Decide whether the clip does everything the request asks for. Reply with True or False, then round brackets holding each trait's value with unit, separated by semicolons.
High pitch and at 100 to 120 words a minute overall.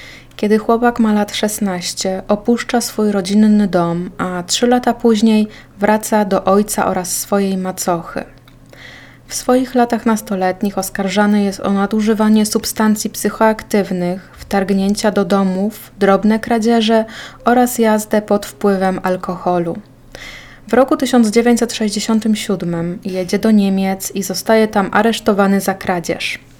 True (205 Hz; 115 wpm)